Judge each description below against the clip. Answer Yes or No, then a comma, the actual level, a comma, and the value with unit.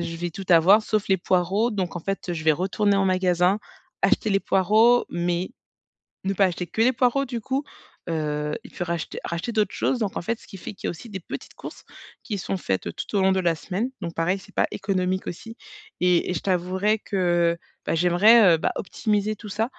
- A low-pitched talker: No, high, 190 Hz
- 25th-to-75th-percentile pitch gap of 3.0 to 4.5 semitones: Yes, average, 3.4 semitones